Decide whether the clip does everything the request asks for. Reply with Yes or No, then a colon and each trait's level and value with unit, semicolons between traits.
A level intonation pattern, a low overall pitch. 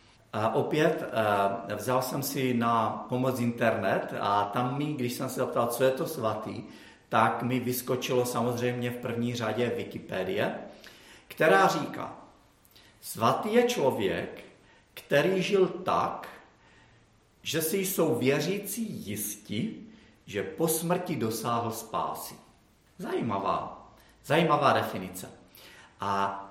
No: average, 4.6 semitones; low, 125 Hz